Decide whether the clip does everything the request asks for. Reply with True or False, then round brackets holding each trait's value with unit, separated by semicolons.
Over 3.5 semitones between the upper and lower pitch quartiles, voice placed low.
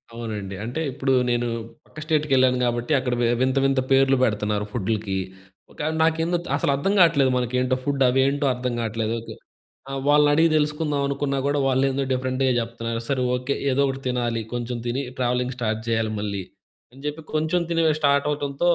False (3.2 semitones; 130 Hz)